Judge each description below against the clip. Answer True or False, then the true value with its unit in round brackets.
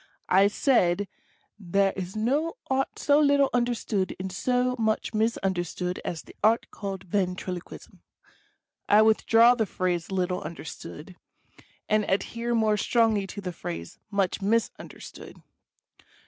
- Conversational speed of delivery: False (130 wpm)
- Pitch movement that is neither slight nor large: True (4.0 semitones)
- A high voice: True (205 Hz)